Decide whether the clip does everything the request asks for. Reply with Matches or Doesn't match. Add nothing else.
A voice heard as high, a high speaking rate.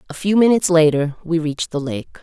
Doesn't match